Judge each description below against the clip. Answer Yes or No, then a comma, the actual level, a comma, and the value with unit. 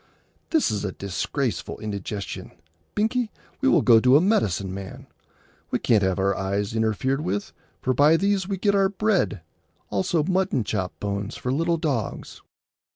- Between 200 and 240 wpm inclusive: No, average, 155 wpm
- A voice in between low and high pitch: No, low, 125 Hz